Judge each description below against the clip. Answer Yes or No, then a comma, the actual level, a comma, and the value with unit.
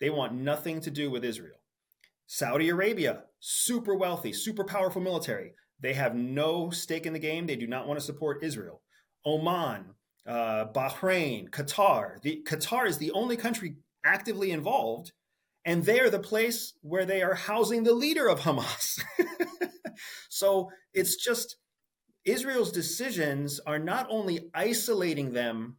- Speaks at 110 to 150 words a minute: Yes, average, 145 wpm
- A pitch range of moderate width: No, wide, 6.7 semitones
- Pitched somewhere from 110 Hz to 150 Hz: No, medium, 170 Hz